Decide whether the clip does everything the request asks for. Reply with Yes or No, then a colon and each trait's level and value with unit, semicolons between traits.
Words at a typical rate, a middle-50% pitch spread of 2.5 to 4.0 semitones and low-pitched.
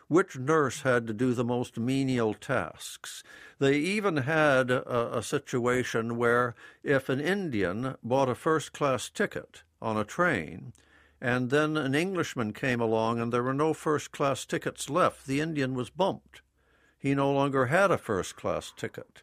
Yes: average, 165 wpm; average, 3.4 semitones; low, 130 Hz